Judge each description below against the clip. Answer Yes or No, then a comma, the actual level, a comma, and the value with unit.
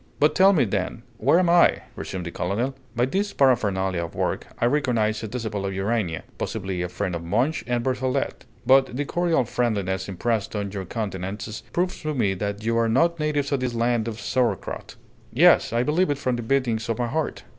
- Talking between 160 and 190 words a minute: No, average, 200 wpm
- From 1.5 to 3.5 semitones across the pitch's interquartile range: No, average, 5.2 semitones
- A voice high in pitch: No, low, 115 Hz